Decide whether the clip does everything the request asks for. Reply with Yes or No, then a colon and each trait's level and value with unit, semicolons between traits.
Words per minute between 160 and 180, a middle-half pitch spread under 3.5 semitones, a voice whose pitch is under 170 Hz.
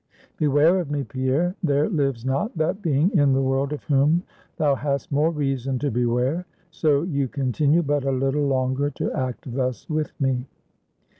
Yes: average, 170 wpm; narrow, 2.5 semitones; medium, 140 Hz